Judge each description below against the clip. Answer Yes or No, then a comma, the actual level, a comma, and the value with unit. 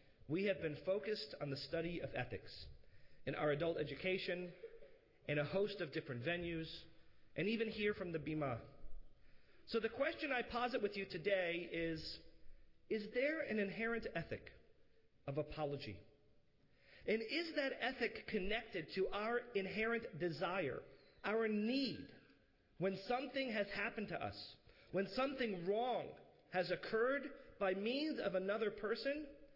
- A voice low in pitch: No, high, 195 Hz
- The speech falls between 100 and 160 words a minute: Yes, average, 140 wpm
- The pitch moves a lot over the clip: Yes, wide, 6.2 semitones